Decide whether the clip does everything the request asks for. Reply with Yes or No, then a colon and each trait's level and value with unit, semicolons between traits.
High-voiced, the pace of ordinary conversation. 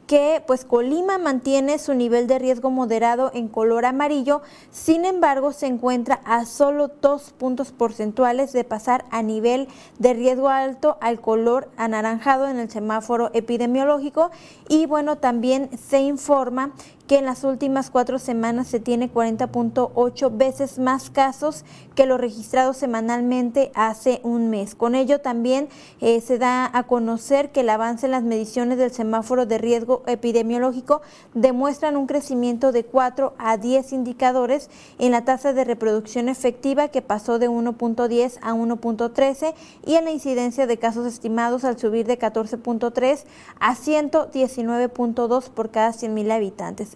Yes: very high, 250 Hz; average, 145 wpm